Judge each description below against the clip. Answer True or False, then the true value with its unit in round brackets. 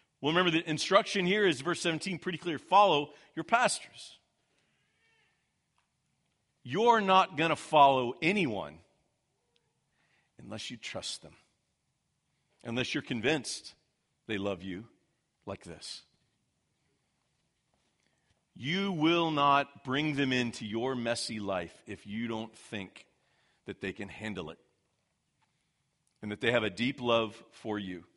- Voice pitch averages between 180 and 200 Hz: False (140 Hz)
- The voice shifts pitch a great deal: True (6.4 semitones)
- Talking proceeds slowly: True (125 wpm)